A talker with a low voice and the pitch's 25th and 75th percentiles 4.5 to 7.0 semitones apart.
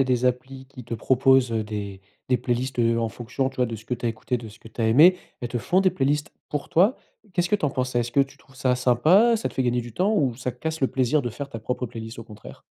No: low, 125 Hz; average, 2.9 semitones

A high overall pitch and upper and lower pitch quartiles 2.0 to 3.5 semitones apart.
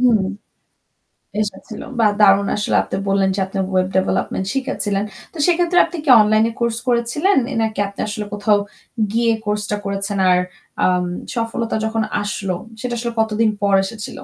Yes: high, 215 Hz; average, 2.8 semitones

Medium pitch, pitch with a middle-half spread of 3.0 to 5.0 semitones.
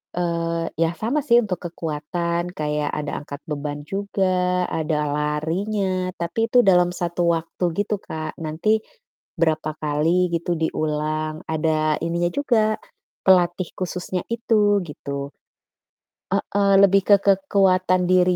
Yes: medium, 175 Hz; average, 3.5 semitones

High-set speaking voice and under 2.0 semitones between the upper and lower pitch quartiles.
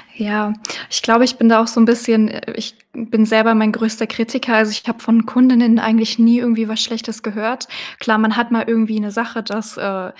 Yes: high, 225 Hz; narrow, 1.0 semitones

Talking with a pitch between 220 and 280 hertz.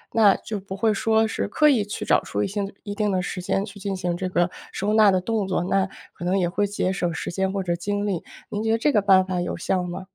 No: high, 195 Hz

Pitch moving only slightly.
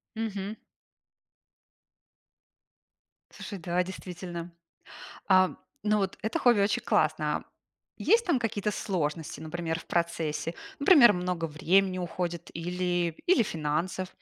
No: average, 3.3 semitones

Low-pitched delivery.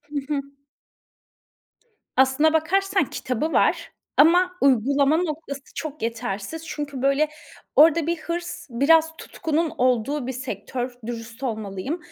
No: very high, 285 Hz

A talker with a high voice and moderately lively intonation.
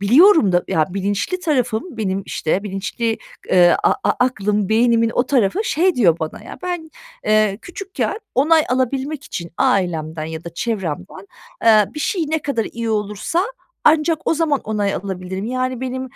No: high, 225 Hz; wide, 6.7 semitones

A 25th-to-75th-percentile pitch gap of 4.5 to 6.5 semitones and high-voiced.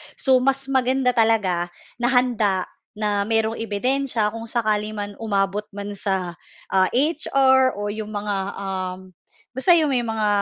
No: average, 3.8 semitones; high, 220 Hz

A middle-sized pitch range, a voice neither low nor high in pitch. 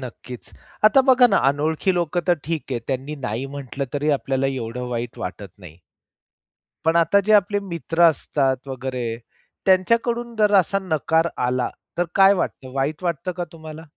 No: wide, 5.8 semitones; medium, 155 Hz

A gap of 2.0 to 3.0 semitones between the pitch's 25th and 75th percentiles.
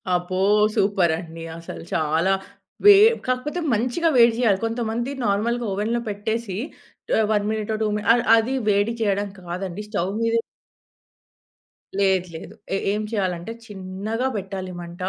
No: average, 3.4 semitones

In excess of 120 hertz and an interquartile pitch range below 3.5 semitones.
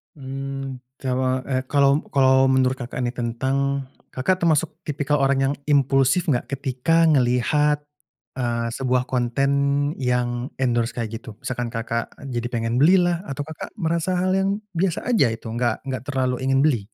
Yes: low, 130 Hz; average, 2.8 semitones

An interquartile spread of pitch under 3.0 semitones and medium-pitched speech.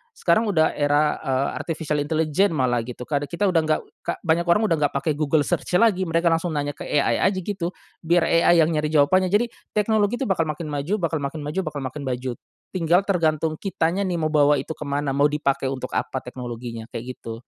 No: average, 3.4 semitones; medium, 155 Hz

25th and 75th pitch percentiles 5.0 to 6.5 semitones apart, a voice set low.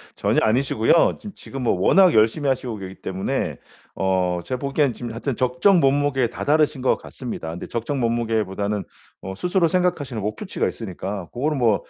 Yes: average, 5.3 semitones; low, 120 Hz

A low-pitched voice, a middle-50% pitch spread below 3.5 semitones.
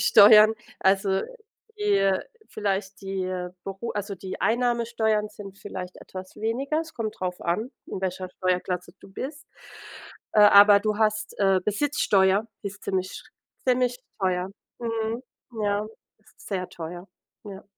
No: high, 205 Hz; average, 2.8 semitones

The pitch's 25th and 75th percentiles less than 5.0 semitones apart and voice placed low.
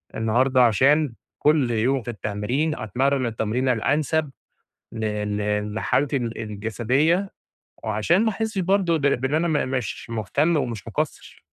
No: wide, 5.6 semitones; low, 130 Hz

